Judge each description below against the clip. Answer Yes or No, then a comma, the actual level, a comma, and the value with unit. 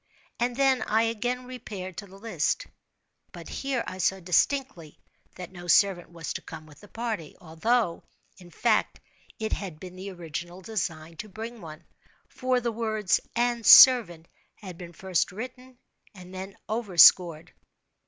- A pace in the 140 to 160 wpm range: Yes, average, 145 wpm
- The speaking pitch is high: Yes, high, 195 Hz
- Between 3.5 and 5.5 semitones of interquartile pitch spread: Yes, average, 5.2 semitones